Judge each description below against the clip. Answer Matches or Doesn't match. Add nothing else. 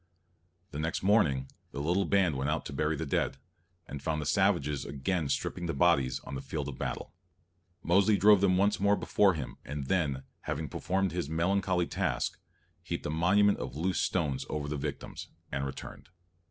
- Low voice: Matches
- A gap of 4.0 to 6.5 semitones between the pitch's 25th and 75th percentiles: Matches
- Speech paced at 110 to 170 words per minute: Doesn't match